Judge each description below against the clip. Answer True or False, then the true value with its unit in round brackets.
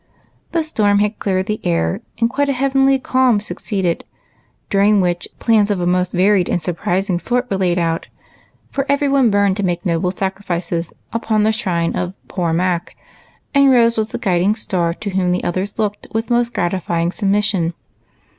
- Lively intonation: False (4.2 semitones)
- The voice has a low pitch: False (200 Hz)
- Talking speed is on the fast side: False (175 wpm)